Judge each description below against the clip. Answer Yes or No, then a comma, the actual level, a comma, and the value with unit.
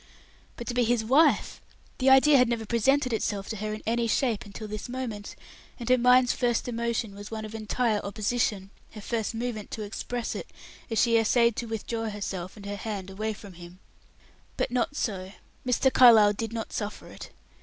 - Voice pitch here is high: Yes, high, 225 Hz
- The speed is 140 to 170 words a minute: No, average, 190 wpm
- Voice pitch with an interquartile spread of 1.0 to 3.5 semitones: Yes, average, 2.7 semitones